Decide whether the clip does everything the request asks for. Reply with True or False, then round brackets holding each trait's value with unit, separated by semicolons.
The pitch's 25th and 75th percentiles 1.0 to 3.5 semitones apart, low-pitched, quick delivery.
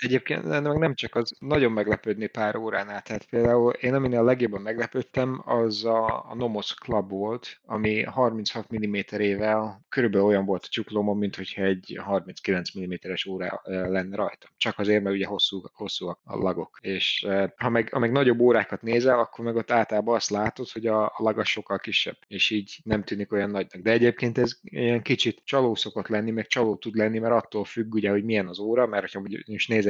True (2.6 semitones; 110 Hz; 195 wpm)